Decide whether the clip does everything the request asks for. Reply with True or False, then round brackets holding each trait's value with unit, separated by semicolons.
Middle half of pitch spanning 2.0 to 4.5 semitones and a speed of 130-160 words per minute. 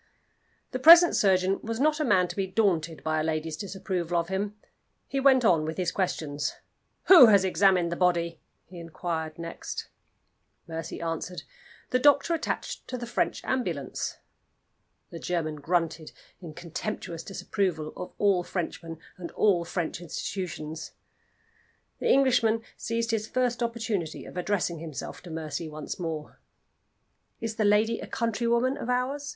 False (5.6 semitones; 145 wpm)